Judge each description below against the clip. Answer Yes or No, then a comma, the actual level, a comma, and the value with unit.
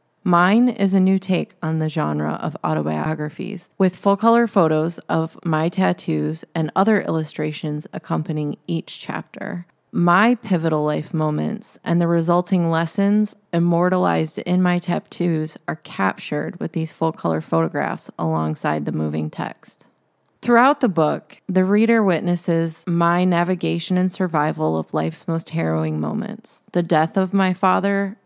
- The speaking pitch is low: No, medium, 170 Hz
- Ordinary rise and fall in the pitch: Yes, average, 3.5 semitones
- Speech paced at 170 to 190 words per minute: No, average, 140 wpm